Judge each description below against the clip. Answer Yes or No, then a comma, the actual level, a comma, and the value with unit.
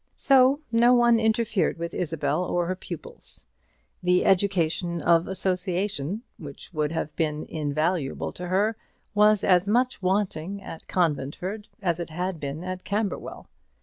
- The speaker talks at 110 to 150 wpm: Yes, average, 140 wpm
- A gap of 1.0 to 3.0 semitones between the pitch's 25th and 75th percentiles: No, average, 4.1 semitones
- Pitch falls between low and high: Yes, medium, 180 Hz